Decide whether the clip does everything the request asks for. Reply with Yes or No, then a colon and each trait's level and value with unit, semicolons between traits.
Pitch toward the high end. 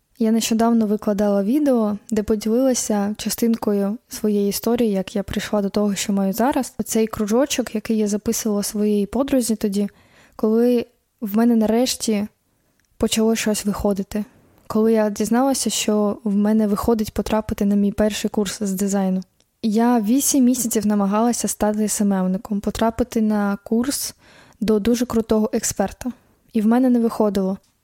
Yes: high, 220 Hz